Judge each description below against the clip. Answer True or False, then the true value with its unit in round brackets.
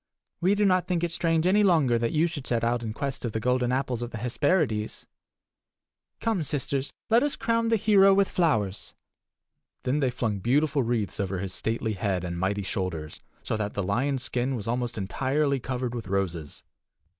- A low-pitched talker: True (125 Hz)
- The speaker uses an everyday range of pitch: False (6.8 semitones)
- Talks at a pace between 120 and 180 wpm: False (190 wpm)